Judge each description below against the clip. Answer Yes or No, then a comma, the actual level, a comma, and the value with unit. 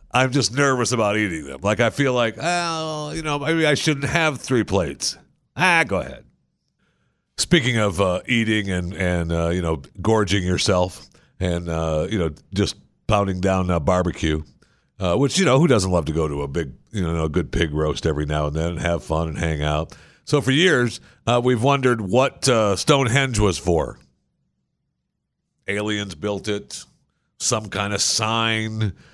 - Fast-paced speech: No, average, 180 wpm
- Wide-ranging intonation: Yes, wide, 6.8 semitones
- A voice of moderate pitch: No, low, 105 Hz